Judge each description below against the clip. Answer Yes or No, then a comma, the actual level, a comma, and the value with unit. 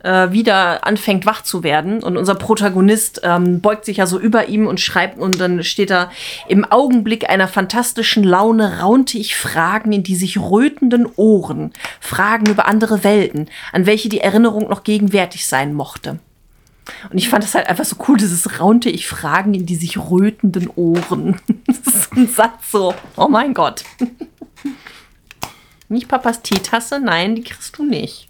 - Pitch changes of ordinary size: Yes, average, 3.4 semitones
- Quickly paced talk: No, average, 165 wpm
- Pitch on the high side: Yes, high, 210 Hz